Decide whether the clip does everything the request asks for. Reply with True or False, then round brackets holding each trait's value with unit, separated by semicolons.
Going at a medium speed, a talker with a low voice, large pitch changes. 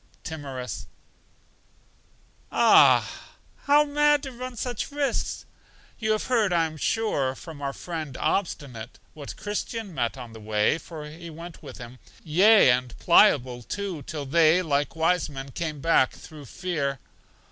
False (145 wpm; 160 Hz; 6.9 semitones)